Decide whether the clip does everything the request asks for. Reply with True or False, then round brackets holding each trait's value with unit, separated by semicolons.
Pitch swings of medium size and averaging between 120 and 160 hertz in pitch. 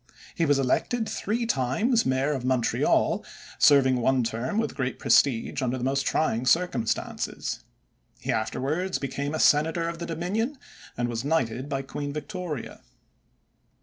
True (4.7 semitones; 140 Hz)